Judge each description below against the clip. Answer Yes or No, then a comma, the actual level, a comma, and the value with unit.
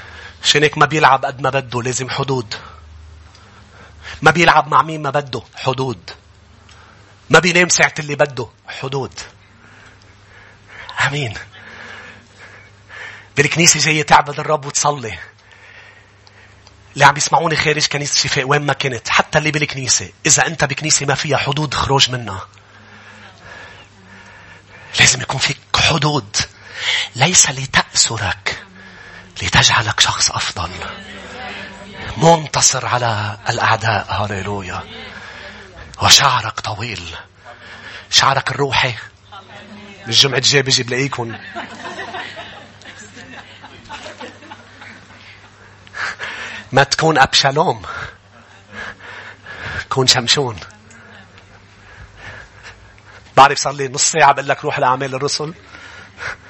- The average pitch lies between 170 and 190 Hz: No, low, 115 Hz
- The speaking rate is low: Yes, slow, 85 wpm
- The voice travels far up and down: Yes, wide, 5.7 semitones